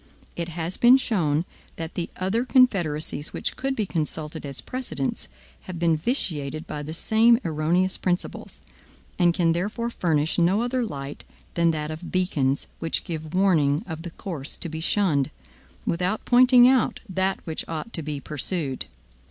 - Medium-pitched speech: Yes, medium, 170 Hz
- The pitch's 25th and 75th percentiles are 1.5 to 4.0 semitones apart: No, average, 4.4 semitones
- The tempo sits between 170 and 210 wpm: No, average, 160 wpm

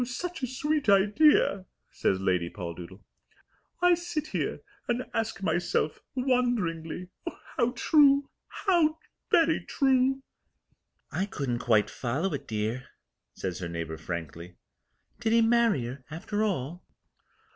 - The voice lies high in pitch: Yes, high, 195 Hz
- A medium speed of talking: No, slow, 120 wpm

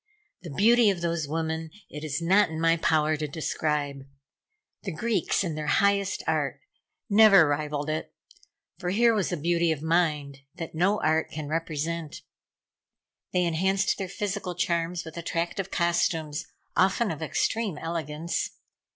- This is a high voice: No, medium, 165 Hz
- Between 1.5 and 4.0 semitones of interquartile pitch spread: Yes, average, 3.4 semitones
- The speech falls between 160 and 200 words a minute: No, average, 145 wpm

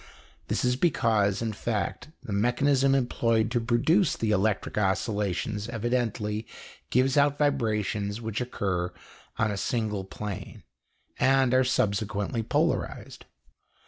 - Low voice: Yes, low, 115 Hz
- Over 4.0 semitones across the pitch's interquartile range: No, average, 3.5 semitones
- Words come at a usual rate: No, slow, 115 wpm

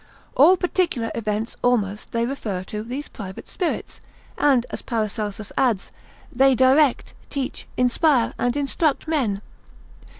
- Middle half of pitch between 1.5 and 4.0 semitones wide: No, average, 4.6 semitones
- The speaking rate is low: Yes, slow, 125 wpm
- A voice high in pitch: Yes, high, 245 Hz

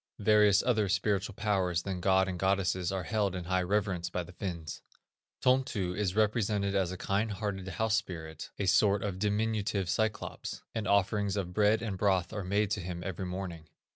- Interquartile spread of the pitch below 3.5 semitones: Yes, narrow, 2.4 semitones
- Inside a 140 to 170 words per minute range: No, average, 180 wpm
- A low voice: Yes, low, 100 Hz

